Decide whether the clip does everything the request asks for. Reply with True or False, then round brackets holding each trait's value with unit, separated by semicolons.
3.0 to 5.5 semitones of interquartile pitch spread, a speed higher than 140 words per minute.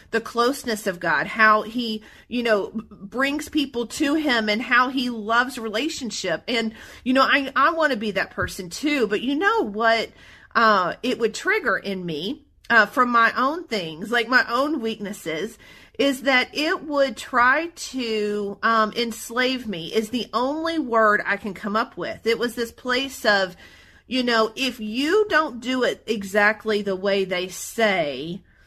True (3.7 semitones; 170 wpm)